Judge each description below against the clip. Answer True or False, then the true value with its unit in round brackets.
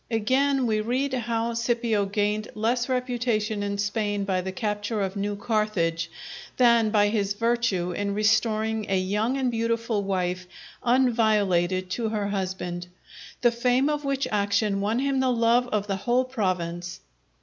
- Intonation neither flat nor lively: True (3.1 semitones)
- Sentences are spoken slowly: False (150 wpm)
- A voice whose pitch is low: False (215 Hz)